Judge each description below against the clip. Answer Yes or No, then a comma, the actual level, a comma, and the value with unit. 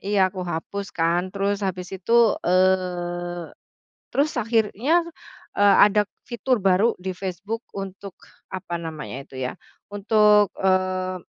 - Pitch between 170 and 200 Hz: Yes, high, 190 Hz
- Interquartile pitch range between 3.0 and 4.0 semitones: No, narrow, 2.5 semitones